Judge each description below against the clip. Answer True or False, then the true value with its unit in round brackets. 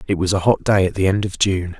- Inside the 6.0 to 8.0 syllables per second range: True (6.1 syllables/s)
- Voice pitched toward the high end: False (95 Hz)